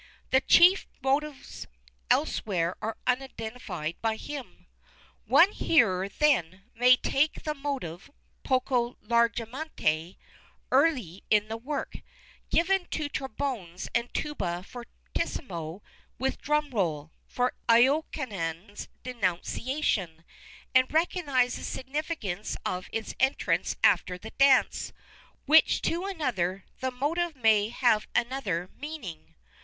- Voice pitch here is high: Yes, high, 245 Hz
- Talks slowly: Yes, slow, 105 wpm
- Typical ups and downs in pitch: No, wide, 6.9 semitones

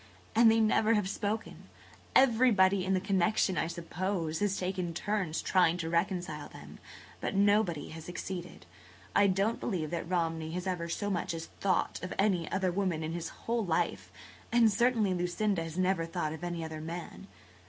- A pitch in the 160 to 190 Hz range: Yes, medium, 185 Hz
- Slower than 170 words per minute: No, average, 180 wpm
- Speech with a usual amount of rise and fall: Yes, average, 3.3 semitones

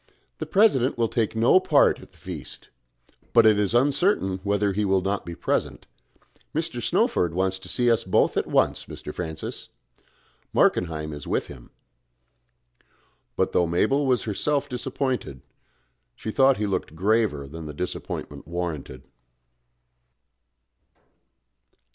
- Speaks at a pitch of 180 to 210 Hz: No, low, 100 Hz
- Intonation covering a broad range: Yes, wide, 5.9 semitones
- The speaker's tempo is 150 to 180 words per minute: No, slow, 135 wpm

